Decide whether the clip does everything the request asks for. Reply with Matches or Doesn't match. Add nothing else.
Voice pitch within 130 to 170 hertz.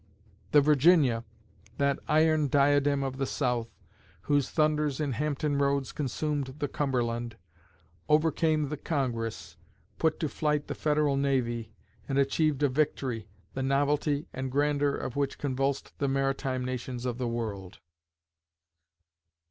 Matches